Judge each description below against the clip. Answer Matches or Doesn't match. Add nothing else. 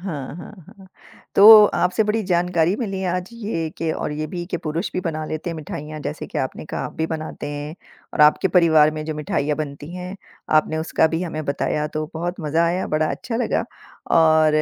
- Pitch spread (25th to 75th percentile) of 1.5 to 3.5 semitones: Matches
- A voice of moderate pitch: Matches